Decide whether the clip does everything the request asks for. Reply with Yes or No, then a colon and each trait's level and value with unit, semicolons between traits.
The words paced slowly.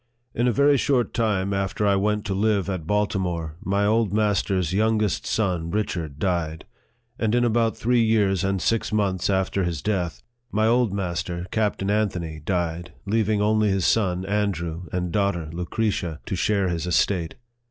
No: average, 165 wpm